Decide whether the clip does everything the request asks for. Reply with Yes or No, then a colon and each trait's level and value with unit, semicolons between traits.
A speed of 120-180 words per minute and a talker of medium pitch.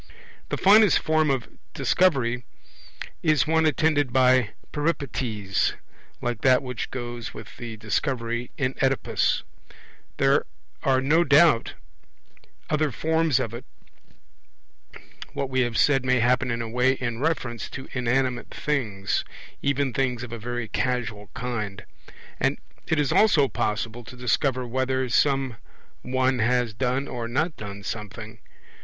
No: slow, 135 wpm; low, 125 Hz